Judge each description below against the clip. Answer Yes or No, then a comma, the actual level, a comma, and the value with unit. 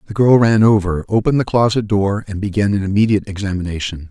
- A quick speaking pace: No, average, 190 wpm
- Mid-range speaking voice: No, low, 100 Hz